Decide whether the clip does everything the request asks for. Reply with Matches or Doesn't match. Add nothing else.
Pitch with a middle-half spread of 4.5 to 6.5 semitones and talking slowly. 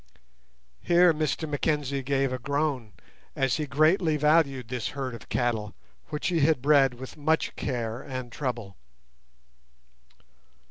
Doesn't match